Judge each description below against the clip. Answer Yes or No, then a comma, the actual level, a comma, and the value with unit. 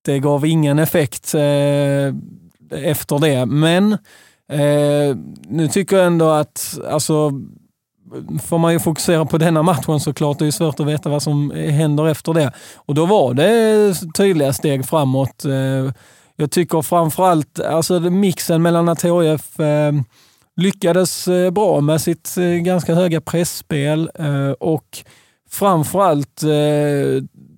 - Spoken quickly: No, average, 140 wpm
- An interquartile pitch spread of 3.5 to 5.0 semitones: No, average, 2.9 semitones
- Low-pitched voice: No, medium, 155 Hz